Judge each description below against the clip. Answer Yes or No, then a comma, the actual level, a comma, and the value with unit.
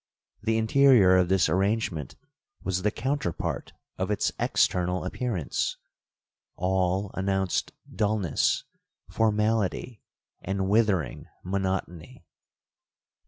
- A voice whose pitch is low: Yes, very low, 95 Hz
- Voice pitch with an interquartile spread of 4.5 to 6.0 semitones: No, average, 3.1 semitones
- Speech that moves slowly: Yes, slow, 80 wpm